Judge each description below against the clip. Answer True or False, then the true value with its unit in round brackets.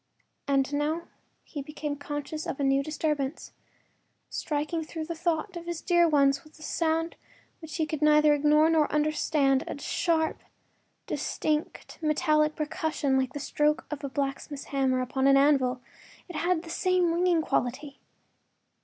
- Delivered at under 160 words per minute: True (150 wpm)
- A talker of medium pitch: False (300 Hz)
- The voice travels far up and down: False (2.4 semitones)